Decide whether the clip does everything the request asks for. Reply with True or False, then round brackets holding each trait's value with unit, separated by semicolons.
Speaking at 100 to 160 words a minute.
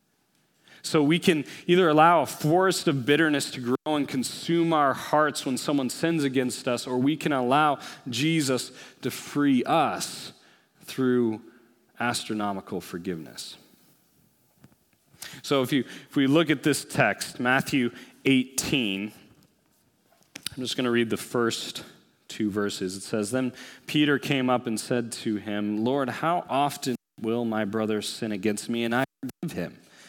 True (150 wpm)